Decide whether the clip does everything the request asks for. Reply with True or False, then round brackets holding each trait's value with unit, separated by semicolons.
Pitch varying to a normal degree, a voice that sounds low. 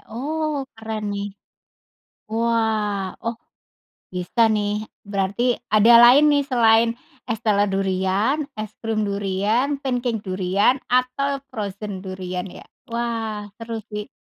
False (3.0 semitones; 220 Hz)